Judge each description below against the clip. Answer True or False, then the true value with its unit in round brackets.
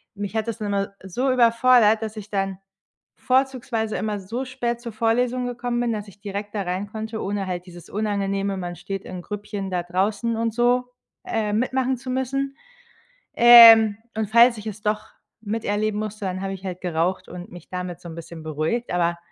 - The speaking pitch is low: False (210 Hz)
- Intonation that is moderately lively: True (3.4 semitones)